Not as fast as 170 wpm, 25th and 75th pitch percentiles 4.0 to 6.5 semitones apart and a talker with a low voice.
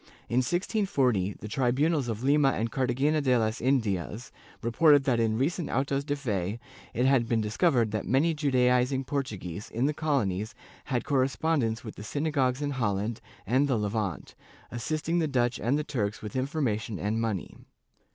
Yes: average, 160 wpm; average, 4.3 semitones; low, 125 Hz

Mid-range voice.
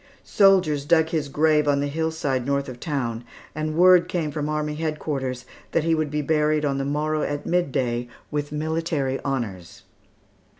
Yes: medium, 150 Hz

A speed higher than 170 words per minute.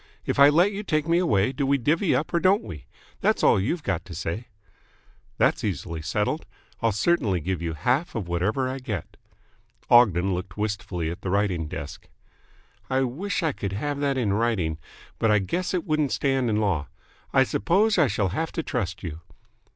Yes: average, 190 wpm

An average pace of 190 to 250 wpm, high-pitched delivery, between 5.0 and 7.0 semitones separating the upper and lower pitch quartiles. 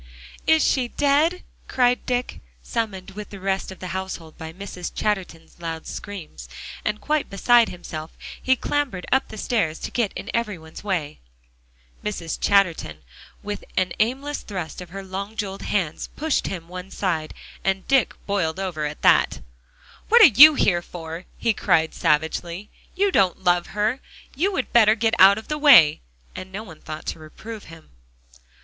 No: average, 170 wpm; high, 195 Hz; wide, 5.4 semitones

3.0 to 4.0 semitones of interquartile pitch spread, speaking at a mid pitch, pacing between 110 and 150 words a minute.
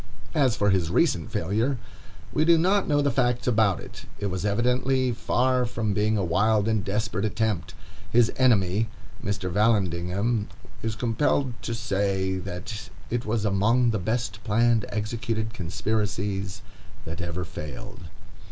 No: average, 3.5 semitones; low, 110 Hz; average, 145 wpm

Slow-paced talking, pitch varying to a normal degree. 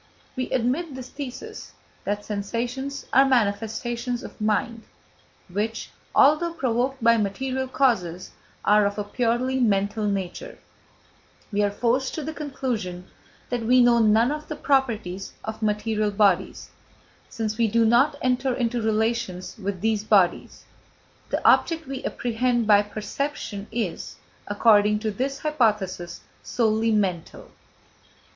Yes: slow, 130 wpm; average, 3.8 semitones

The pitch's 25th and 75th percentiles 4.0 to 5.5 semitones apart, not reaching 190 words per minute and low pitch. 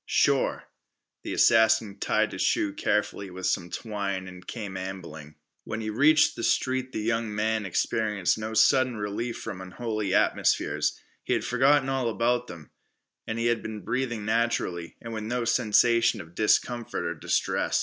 No: average, 3.0 semitones; average, 160 wpm; low, 110 Hz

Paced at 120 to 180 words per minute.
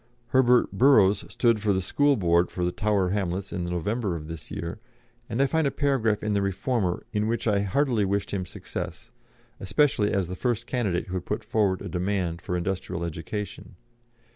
No: average, 190 wpm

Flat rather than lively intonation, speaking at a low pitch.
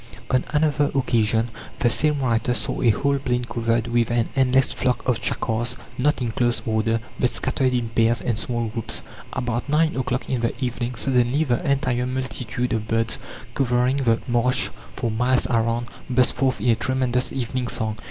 Yes: narrow, 1.9 semitones; low, 125 Hz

